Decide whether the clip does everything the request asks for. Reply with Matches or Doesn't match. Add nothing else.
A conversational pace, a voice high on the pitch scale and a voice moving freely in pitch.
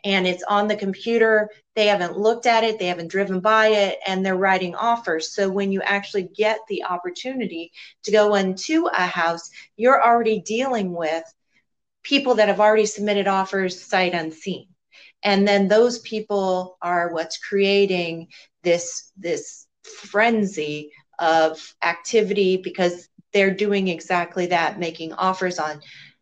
Doesn't match